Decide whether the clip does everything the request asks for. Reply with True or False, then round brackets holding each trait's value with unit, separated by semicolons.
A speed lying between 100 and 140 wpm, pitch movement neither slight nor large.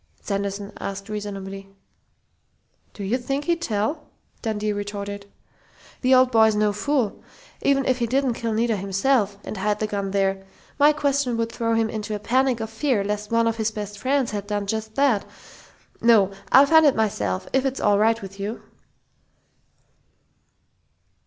False (165 wpm; 3.9 semitones)